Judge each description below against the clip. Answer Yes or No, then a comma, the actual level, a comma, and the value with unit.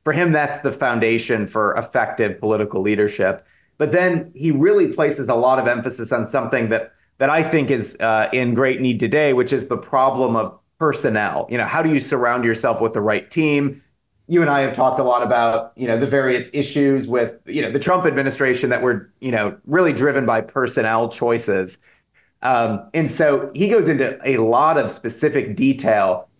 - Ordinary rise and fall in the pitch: Yes, average, 4.1 semitones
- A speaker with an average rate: Yes, average, 195 wpm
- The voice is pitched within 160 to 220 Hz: No, low, 130 Hz